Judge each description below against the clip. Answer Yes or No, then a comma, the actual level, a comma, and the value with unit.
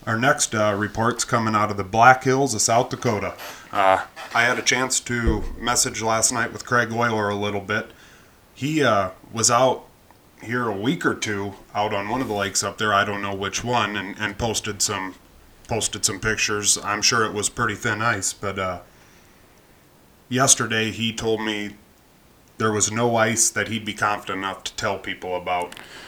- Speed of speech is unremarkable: Yes, average, 190 wpm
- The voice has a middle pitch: No, low, 105 Hz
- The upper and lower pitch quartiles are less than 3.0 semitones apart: Yes, narrow, 2.6 semitones